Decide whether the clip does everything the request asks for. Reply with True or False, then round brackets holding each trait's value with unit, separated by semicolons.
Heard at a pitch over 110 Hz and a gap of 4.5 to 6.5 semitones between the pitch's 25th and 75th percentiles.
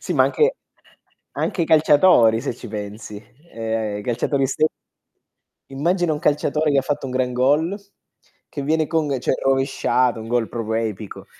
True (135 Hz; 5.1 semitones)